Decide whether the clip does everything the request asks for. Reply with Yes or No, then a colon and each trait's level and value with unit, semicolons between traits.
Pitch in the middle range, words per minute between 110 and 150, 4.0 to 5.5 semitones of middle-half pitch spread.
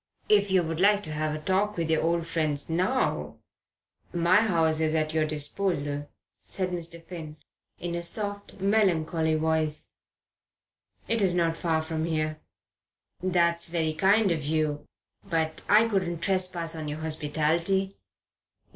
No: medium, 165 Hz; average, 145 wpm; average, 3.1 semitones